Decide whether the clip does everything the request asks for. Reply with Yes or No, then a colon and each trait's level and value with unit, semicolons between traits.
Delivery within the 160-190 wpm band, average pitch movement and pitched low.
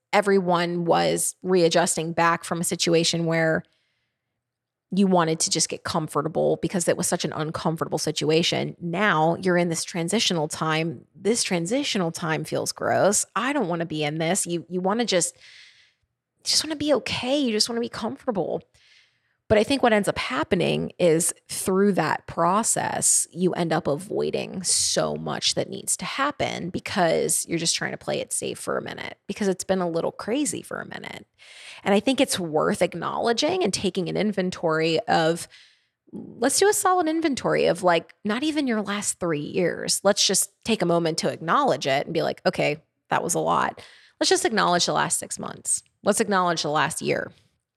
No: average, 185 wpm; average, 4.4 semitones; medium, 180 Hz